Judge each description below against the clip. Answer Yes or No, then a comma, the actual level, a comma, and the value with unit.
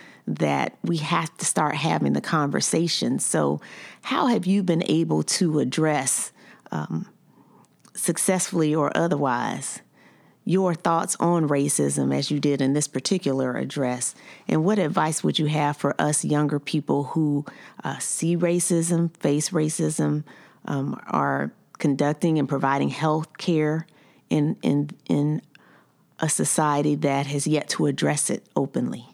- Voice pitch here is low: No, medium, 150 Hz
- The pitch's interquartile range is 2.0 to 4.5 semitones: Yes, average, 2.8 semitones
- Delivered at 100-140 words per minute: Yes, slow, 135 wpm